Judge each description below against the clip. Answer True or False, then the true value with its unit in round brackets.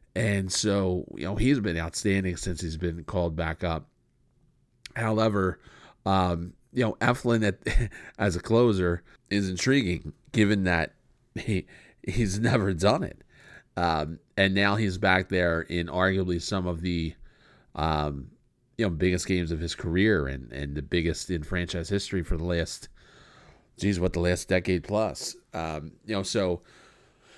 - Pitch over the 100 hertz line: False (90 Hz)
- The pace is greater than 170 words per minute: False (155 wpm)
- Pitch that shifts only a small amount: False (3.3 semitones)